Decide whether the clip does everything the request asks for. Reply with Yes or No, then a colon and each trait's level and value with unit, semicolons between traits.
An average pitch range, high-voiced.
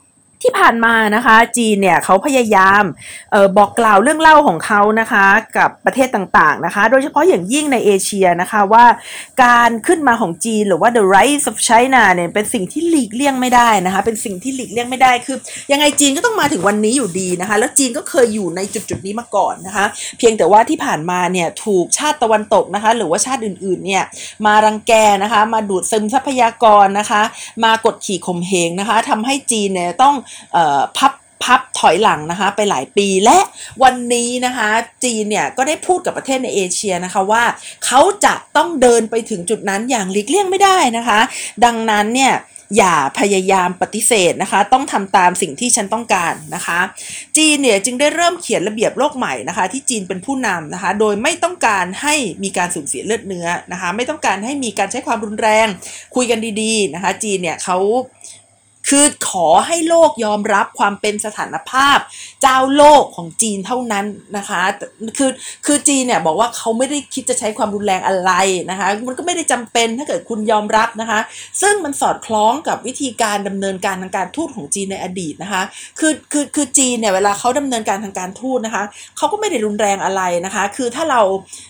Yes: average, 4.8 semitones; high, 225 Hz